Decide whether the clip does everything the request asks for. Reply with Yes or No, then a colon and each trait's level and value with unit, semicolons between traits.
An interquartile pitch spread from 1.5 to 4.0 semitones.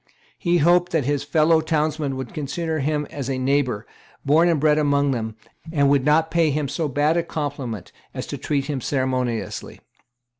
Yes: average, 2.7 semitones